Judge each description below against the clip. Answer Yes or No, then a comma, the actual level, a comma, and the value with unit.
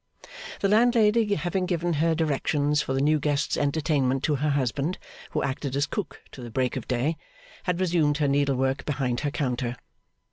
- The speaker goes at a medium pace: Yes, average, 175 wpm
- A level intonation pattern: No, average, 3.7 semitones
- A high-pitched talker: No, medium, 145 Hz